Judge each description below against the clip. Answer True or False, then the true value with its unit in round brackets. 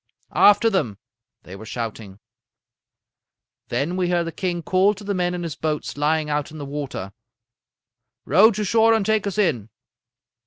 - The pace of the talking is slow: False (165 wpm)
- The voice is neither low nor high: True (170 Hz)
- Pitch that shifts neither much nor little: False (5.7 semitones)